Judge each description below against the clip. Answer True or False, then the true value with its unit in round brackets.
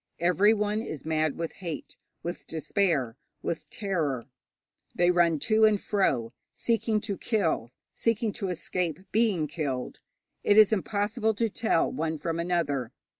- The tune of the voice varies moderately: True (5.0 semitones)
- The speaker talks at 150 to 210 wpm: False (135 wpm)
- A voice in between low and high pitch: True (180 Hz)